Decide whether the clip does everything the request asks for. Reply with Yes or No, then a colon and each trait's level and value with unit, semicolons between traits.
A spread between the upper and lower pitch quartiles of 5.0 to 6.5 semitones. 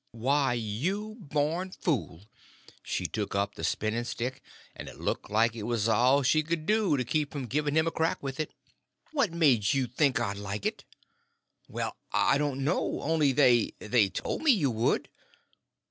Yes: average, 5.3 semitones